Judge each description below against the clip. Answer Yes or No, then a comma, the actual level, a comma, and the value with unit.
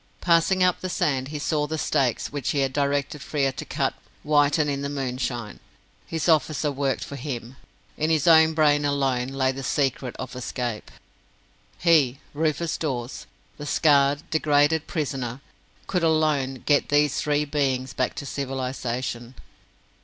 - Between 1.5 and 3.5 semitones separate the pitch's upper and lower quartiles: Yes, narrow, 2.6 semitones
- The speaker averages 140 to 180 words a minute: Yes, average, 150 wpm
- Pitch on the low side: No, medium, 145 Hz